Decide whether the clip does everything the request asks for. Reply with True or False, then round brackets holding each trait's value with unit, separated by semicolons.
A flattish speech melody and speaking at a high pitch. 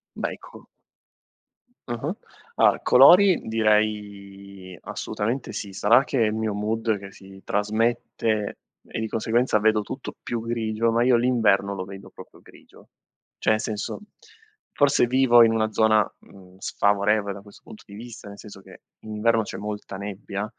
False (2.2 semitones; 110 Hz)